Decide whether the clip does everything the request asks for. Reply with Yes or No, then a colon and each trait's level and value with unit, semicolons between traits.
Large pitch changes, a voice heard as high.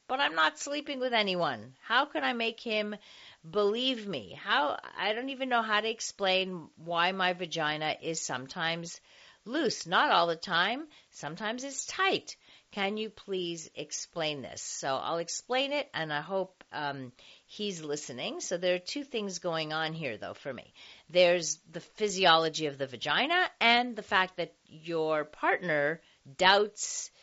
No: wide, 5.7 semitones; medium, 180 Hz